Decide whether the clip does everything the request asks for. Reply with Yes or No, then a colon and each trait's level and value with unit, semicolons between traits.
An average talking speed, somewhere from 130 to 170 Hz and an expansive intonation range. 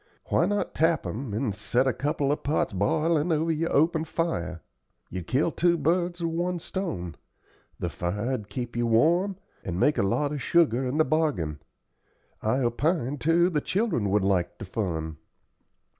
Yes: average, 170 wpm; medium, 140 Hz; wide, 8.1 semitones